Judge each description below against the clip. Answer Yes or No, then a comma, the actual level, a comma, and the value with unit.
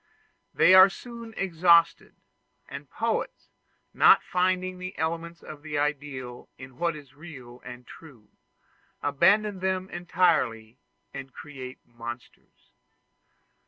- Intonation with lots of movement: Yes, wide, 5.9 semitones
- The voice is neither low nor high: Yes, medium, 160 Hz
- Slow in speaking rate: Yes, slow, 110 wpm